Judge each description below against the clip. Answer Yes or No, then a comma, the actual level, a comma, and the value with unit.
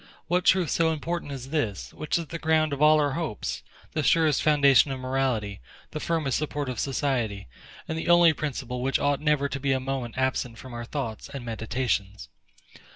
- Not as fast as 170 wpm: No, average, 190 wpm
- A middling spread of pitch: Yes, average, 3.5 semitones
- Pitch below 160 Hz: Yes, medium, 140 Hz